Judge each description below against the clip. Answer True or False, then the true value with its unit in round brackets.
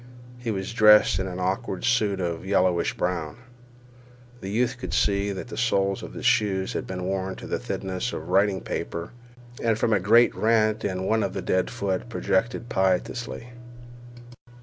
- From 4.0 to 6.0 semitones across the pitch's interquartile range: False (3.2 semitones)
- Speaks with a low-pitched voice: True (100 Hz)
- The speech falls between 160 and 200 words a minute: True (170 wpm)